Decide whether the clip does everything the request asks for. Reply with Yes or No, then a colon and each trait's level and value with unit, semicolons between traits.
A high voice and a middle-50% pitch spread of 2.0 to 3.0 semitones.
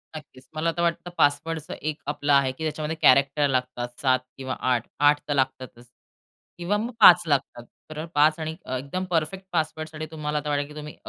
No: medium, 150 Hz; average, 2.7 semitones